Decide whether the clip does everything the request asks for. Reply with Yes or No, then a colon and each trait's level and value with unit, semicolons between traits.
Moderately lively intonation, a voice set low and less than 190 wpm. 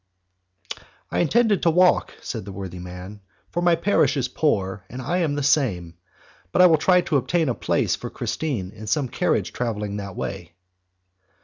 No: wide, 9.0 semitones; low, 130 Hz; average, 180 wpm